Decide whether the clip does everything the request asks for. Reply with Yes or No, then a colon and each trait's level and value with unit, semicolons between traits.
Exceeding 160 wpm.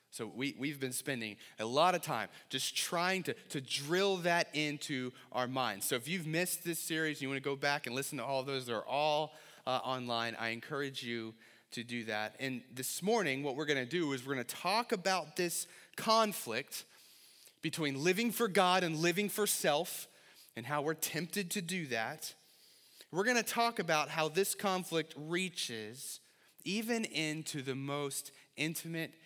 Yes: average, 190 wpm